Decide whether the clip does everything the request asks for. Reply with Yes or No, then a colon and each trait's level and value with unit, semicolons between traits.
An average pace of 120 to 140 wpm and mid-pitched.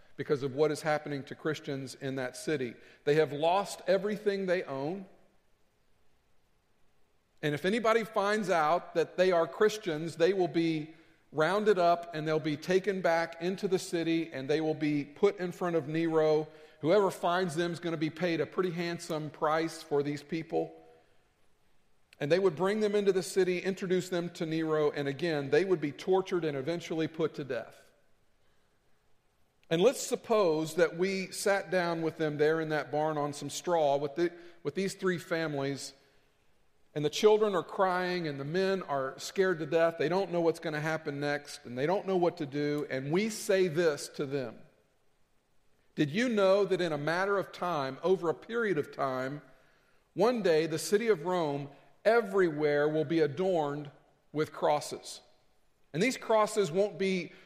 No: average, 180 wpm; medium, 165 Hz